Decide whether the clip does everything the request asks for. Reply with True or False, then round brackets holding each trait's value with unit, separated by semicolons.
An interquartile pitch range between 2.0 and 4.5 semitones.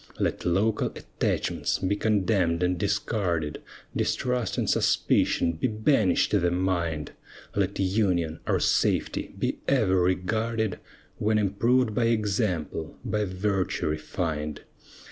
True (3.7 semitones)